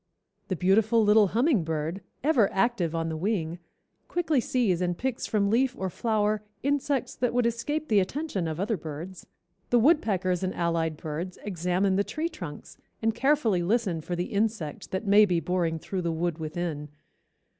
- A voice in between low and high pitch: No, high, 195 Hz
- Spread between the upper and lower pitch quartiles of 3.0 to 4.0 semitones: No, wide, 5.4 semitones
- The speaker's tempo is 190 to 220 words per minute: No, average, 165 wpm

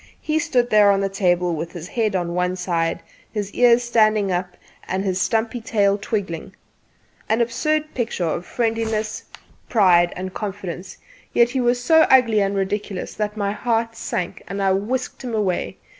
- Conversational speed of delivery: Yes, average, 170 wpm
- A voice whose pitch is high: Yes, high, 210 Hz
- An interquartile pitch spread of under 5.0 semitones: Yes, average, 3.9 semitones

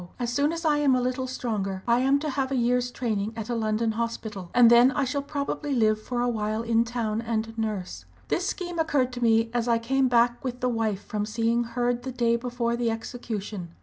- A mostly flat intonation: Yes, narrow, 2.2 semitones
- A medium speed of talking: No, fast, 225 wpm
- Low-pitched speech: No, high, 235 Hz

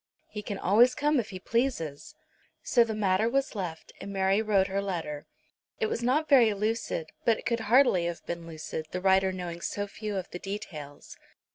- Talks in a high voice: Yes, high, 200 Hz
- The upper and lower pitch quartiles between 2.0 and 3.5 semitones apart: No, average, 4.4 semitones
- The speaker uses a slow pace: No, average, 190 wpm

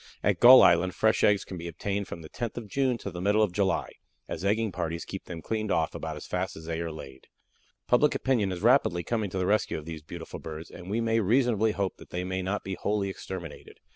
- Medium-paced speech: No, fast, 240 wpm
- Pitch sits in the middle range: No, very low, 95 Hz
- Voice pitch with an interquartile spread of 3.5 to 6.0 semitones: Yes, average, 4.2 semitones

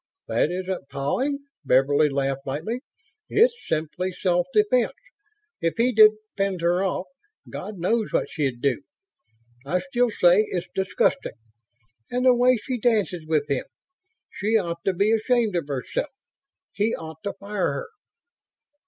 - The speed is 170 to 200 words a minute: No, average, 145 wpm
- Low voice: No, high, 190 Hz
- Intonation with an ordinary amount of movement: No, wide, 6.0 semitones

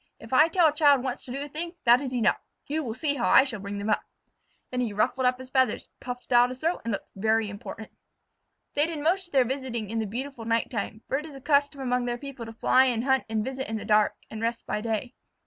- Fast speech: Yes, fast, 260 wpm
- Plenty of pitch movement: No, average, 3.7 semitones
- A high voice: Yes, very high, 250 Hz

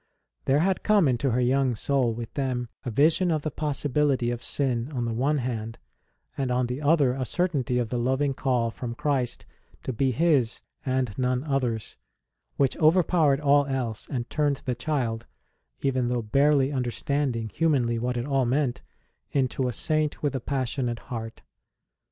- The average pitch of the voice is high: No, low, 130 Hz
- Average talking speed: Yes, average, 175 wpm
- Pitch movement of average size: Yes, average, 3.1 semitones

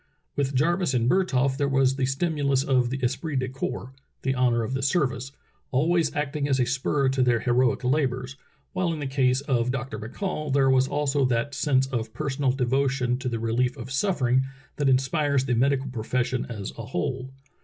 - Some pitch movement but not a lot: No, narrow, 2.0 semitones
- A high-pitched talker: No, low, 130 Hz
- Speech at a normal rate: Yes, average, 195 wpm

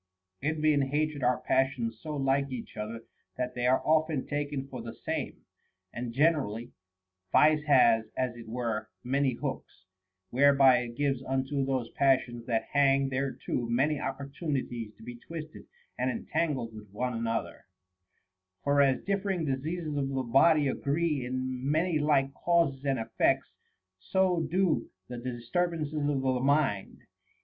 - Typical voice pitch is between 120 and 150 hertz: Yes, low, 135 Hz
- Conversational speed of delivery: Yes, average, 150 wpm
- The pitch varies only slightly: No, average, 3.4 semitones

